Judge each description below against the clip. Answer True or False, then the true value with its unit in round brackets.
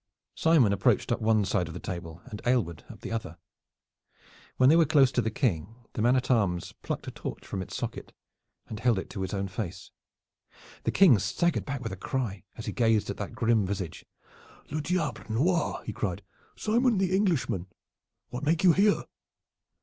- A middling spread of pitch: False (7.5 semitones)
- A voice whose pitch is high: False (115 Hz)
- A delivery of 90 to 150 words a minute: False (190 wpm)